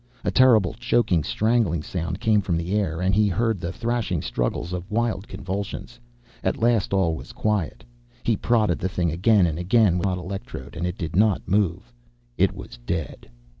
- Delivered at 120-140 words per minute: No, average, 185 wpm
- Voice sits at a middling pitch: No, very low, 95 Hz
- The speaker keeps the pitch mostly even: No, average, 4.1 semitones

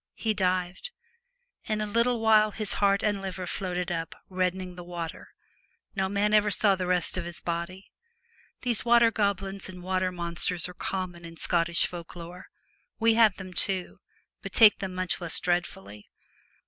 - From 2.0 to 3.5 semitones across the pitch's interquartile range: Yes, average, 2.7 semitones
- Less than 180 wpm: Yes, average, 165 wpm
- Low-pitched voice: No, medium, 185 Hz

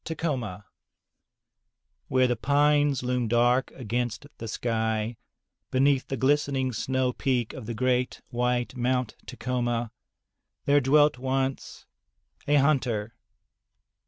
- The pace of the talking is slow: Yes, slow, 115 wpm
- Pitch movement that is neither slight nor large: No, narrow, 2.2 semitones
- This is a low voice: Yes, low, 125 Hz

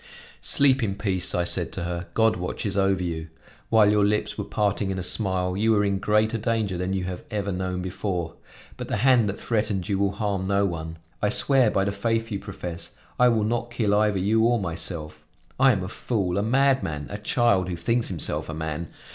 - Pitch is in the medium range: No, low, 100 Hz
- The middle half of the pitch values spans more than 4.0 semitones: No, average, 3.4 semitones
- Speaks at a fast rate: Yes, fast, 215 wpm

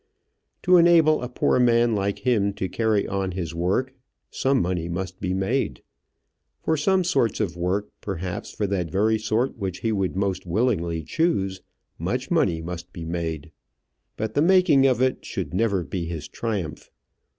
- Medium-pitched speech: No, low, 100 Hz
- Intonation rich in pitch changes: Yes, wide, 5.7 semitones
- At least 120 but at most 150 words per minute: No, average, 165 wpm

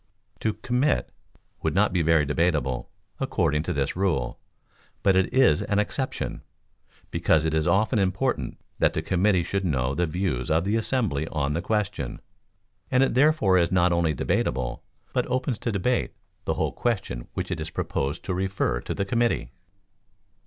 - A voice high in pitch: No, very low, 90 Hz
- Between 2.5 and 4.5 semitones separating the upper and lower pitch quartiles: No, wide, 5.4 semitones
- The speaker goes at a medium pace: Yes, average, 165 wpm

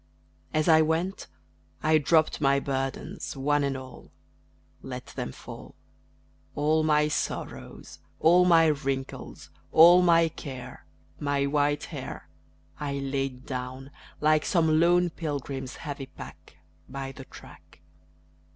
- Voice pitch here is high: No, medium, 145 Hz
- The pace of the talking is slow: Yes, slow, 120 wpm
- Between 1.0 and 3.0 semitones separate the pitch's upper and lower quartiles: Yes, average, 2.7 semitones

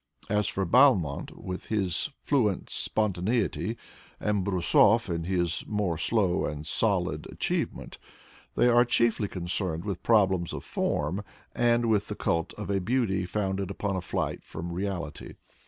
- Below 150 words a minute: Yes, average, 140 wpm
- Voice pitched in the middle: No, very low, 95 Hz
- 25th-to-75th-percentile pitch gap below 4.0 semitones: Yes, average, 3.6 semitones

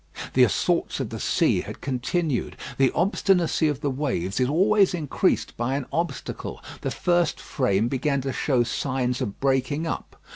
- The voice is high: No, medium, 140 Hz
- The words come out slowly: No, average, 160 wpm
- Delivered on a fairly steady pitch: No, average, 4.5 semitones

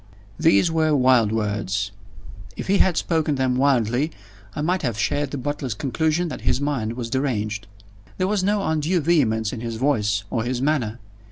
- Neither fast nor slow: Yes, average, 175 wpm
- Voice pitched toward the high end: No, low, 130 Hz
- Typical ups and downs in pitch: No, wide, 5.7 semitones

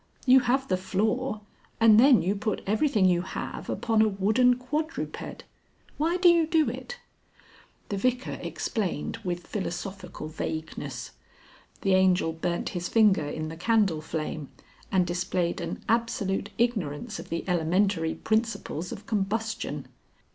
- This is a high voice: Yes, high, 200 Hz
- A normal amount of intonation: Yes, average, 4.8 semitones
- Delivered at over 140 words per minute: No, slow, 135 wpm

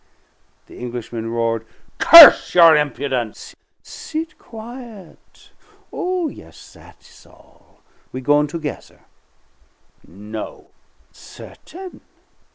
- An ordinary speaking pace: No, slow, 80 wpm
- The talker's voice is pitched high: No, medium, 150 Hz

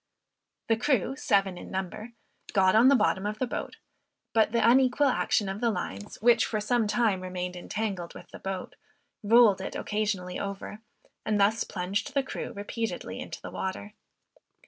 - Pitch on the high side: Yes, high, 210 Hz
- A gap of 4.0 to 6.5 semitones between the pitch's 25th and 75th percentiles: No, average, 3.5 semitones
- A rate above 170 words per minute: No, average, 165 wpm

